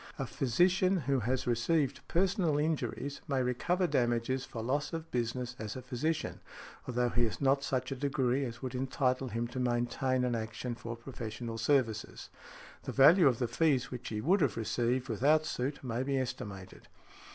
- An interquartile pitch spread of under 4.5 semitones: Yes, average, 2.9 semitones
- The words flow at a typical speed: Yes, average, 175 wpm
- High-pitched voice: No, low, 130 Hz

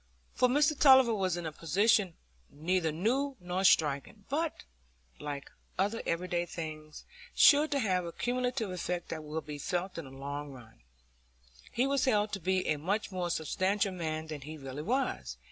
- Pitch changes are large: Yes, wide, 6.1 semitones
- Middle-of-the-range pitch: Yes, medium, 180 Hz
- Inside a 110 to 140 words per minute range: No, average, 170 wpm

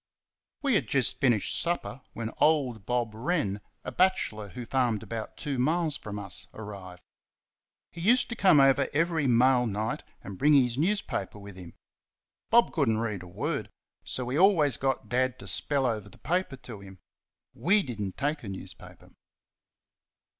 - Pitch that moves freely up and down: Yes, wide, 6.2 semitones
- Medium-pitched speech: No, low, 125 Hz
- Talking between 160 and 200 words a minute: Yes, average, 170 wpm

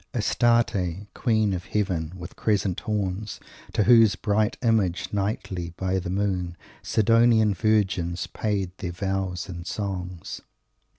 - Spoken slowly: Yes, slow, 120 wpm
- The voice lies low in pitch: Yes, very low, 95 Hz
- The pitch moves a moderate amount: Yes, average, 3.1 semitones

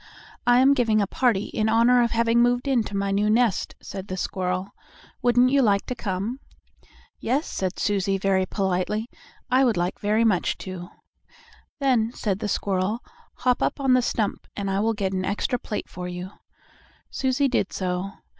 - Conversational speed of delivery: Yes, average, 175 wpm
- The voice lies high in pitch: Yes, high, 210 Hz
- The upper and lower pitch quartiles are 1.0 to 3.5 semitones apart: No, average, 4.2 semitones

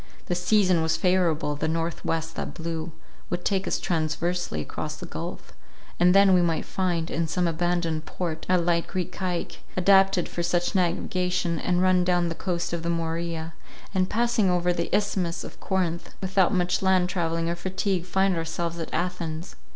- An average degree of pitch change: No, narrow, 1.8 semitones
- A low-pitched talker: No, medium, 175 Hz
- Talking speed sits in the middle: Yes, average, 175 wpm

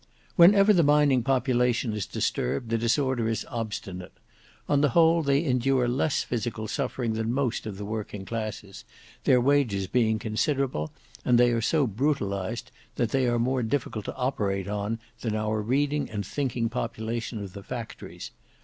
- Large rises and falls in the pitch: No, average, 3.8 semitones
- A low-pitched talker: Yes, low, 120 Hz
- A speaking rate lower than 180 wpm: Yes, average, 160 wpm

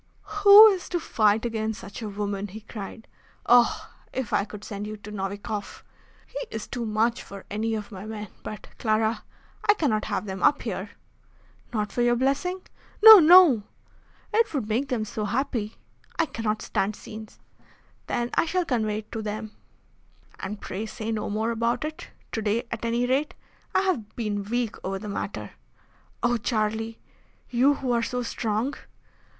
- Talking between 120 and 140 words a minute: No, average, 170 wpm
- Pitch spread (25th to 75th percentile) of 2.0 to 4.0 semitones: Yes, average, 2.9 semitones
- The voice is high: Yes, high, 225 Hz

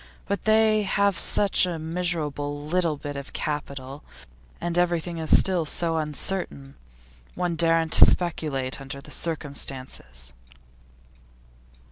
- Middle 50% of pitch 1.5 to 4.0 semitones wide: Yes, average, 3.6 semitones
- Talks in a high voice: No, medium, 160 Hz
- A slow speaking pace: Yes, slow, 110 wpm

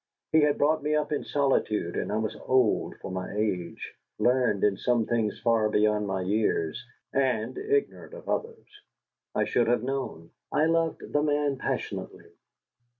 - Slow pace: No, average, 160 wpm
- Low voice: Yes, low, 120 Hz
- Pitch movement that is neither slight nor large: No, wide, 5.8 semitones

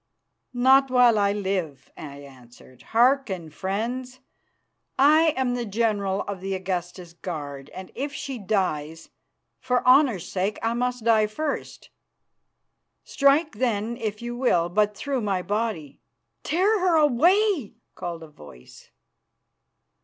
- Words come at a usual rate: No, slow, 125 wpm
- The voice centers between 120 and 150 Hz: No, high, 215 Hz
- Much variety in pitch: Yes, wide, 6.1 semitones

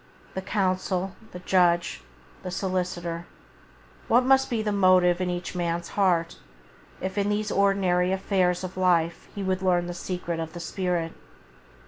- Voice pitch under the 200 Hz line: Yes, medium, 185 Hz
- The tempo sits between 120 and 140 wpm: No, average, 150 wpm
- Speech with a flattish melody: Yes, narrow, 1.7 semitones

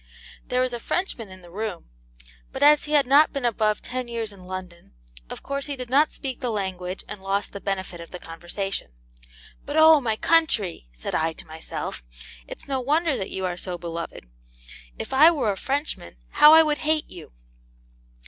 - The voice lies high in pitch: Yes, high, 220 Hz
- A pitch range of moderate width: No, wide, 7.4 semitones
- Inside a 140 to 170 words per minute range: No, average, 195 wpm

